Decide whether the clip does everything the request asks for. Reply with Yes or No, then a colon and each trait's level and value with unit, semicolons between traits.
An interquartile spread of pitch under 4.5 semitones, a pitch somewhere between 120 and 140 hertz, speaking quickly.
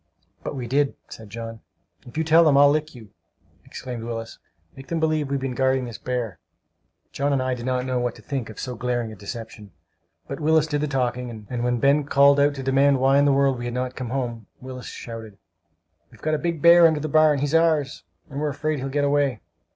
Yes: average, 3.1 semitones; low, 135 Hz; fast, 230 wpm